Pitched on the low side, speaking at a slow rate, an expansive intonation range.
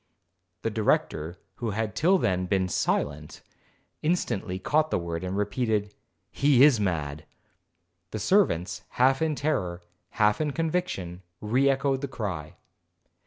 Yes: low, 105 Hz; slow, 130 wpm; wide, 7.3 semitones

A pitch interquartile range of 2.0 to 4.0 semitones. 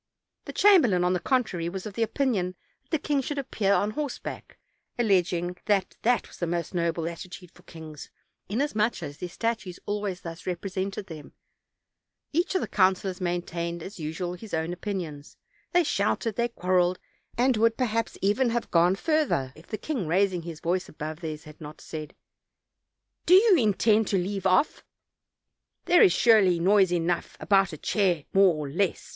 No: average, 4.6 semitones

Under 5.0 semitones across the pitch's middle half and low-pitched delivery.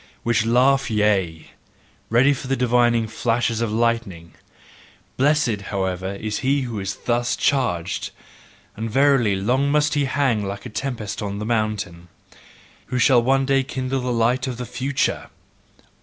Yes: average, 3.9 semitones; low, 120 Hz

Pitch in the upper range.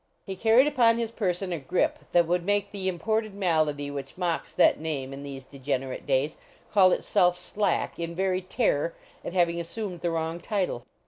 No: medium, 175 Hz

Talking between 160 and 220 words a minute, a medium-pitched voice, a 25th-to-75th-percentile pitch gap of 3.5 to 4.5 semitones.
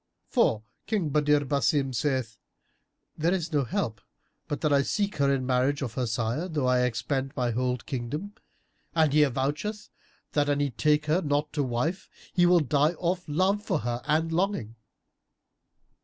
Yes: average, 170 wpm; medium, 145 Hz; average, 4.2 semitones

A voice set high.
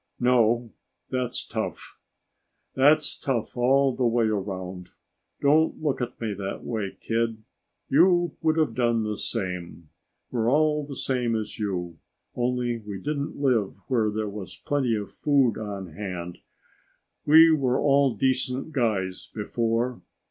No: low, 120 Hz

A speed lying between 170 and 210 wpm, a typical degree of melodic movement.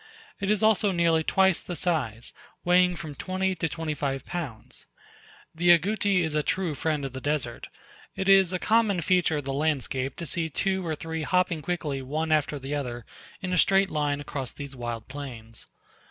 Yes: average, 185 wpm; average, 4.5 semitones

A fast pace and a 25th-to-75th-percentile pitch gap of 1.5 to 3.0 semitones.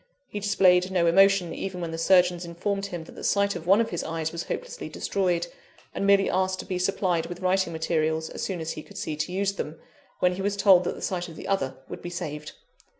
Yes: fast, 240 wpm; average, 2.7 semitones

